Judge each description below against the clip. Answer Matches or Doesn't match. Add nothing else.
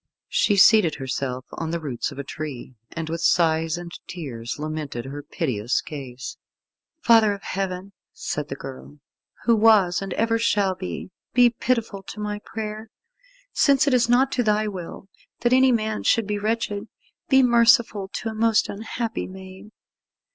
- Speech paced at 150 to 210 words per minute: Matches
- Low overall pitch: Doesn't match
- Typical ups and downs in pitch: Doesn't match